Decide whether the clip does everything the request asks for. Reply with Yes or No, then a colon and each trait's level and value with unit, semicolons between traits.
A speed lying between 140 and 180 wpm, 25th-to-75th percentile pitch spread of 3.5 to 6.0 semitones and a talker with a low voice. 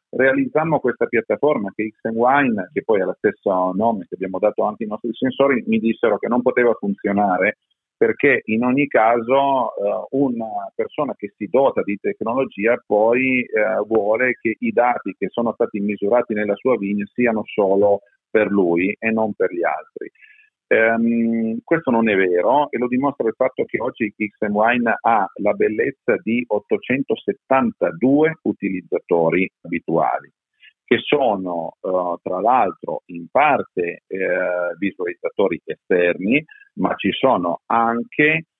Yes: average, 145 wpm; average, 4.6 semitones; low, 115 Hz